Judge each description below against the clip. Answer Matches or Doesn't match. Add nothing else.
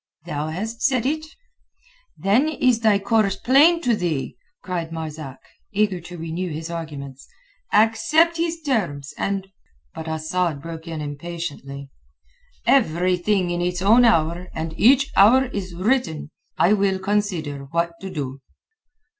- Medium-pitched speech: Matches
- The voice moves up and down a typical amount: Doesn't match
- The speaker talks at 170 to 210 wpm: Doesn't match